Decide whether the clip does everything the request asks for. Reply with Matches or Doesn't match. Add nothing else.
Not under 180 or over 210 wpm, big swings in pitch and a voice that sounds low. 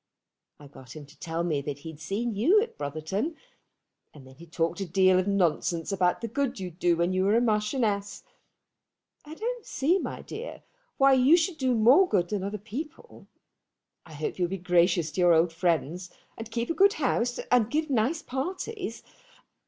Doesn't match